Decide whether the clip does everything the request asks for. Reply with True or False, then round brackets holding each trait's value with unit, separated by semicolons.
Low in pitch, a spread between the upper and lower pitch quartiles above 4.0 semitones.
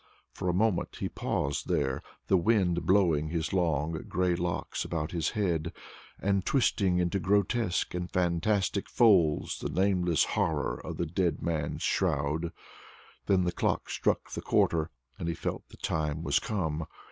False (85 Hz; 3.2 semitones)